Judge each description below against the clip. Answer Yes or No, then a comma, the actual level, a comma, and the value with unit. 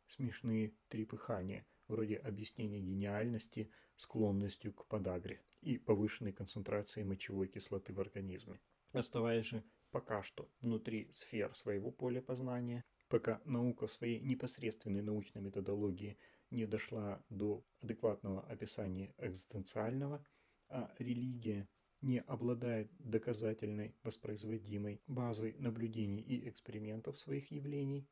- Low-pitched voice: Yes, low, 110 Hz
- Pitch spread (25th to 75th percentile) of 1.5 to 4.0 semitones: Yes, average, 2.8 semitones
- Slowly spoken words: Yes, slow, 105 wpm